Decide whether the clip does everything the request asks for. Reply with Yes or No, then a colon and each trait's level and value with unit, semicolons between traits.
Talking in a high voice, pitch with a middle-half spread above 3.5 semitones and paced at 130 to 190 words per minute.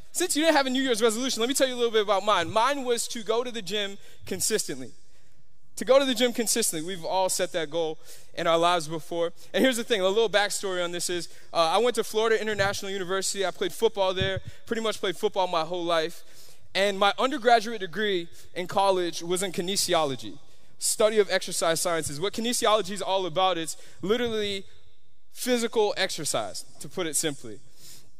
No: high, 195 Hz; average, 4.6 semitones; average, 200 wpm